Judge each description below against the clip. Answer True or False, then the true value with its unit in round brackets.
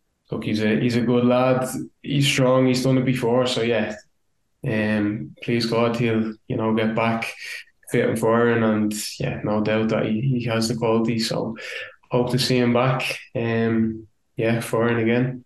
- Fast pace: False (180 wpm)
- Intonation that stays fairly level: True (2.0 semitones)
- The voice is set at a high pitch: False (115 Hz)